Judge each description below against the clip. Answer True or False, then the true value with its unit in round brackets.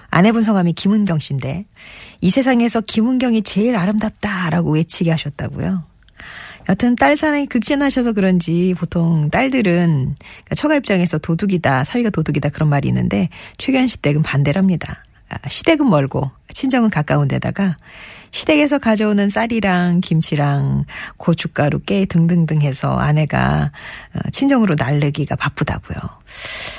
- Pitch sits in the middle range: True (180 Hz)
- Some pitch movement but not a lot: False (6.8 semitones)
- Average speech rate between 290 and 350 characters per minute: True (325 characters per minute)